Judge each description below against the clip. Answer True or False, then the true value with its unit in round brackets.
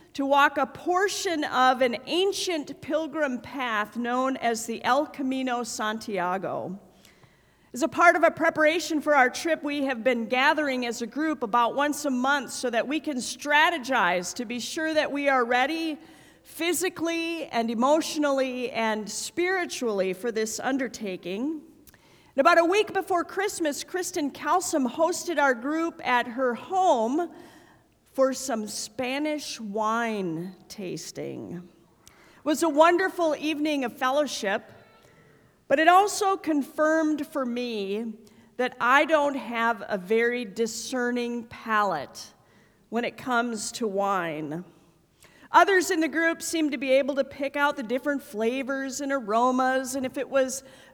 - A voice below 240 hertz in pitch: False (270 Hz)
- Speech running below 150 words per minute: True (140 wpm)